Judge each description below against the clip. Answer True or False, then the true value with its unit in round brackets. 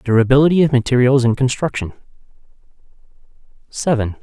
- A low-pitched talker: True (125 Hz)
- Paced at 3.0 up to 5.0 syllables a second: False (6.4 syllables/s)